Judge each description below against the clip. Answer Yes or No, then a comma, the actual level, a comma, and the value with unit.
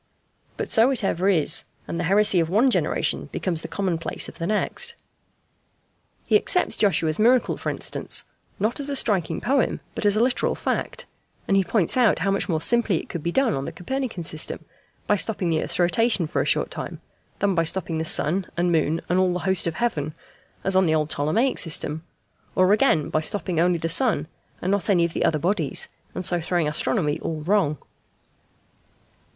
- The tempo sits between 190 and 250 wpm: Yes, average, 200 wpm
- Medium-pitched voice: Yes, medium, 180 Hz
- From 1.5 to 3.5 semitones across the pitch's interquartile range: No, average, 4.5 semitones